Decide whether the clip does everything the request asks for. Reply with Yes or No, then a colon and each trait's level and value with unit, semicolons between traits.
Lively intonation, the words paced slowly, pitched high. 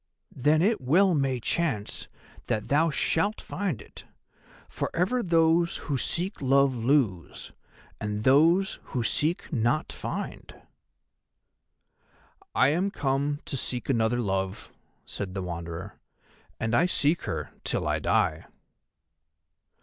No: wide, 6.6 semitones; slow, 120 wpm; medium, 140 Hz